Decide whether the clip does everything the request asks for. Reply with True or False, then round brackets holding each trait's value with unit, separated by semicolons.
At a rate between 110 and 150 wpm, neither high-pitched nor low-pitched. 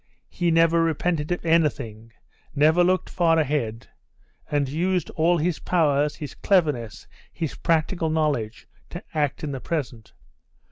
True (135 wpm; 155 Hz)